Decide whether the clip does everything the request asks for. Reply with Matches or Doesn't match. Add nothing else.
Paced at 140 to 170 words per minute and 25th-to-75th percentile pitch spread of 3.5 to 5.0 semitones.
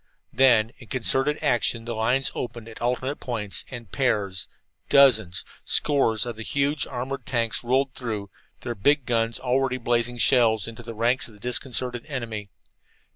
Doesn't match